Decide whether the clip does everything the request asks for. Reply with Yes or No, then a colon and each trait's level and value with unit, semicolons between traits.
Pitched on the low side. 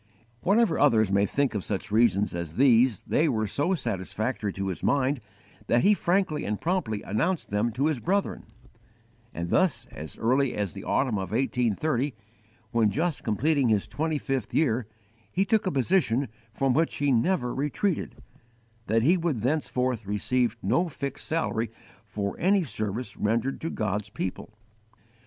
Yes: low, 125 Hz